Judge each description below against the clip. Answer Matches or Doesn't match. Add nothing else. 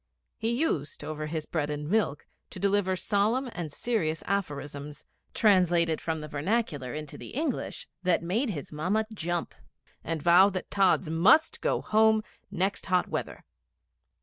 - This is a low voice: Doesn't match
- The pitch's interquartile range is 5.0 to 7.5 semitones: Matches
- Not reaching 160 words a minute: Matches